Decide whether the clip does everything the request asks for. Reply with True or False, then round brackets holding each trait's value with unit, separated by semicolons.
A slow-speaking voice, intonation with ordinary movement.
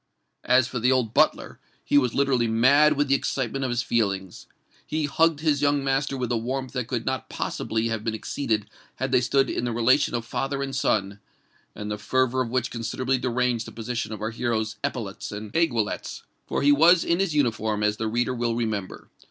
False (200 wpm; 3.3 semitones)